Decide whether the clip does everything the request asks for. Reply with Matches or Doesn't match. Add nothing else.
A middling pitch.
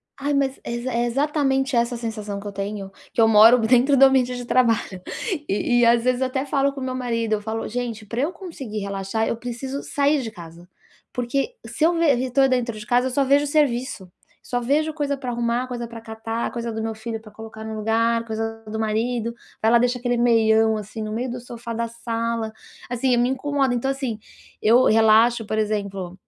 Doesn't match